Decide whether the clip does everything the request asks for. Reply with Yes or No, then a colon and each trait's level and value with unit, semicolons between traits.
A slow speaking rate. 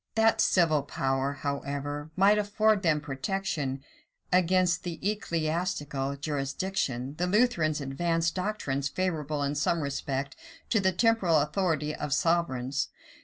Yes: slow, 120 wpm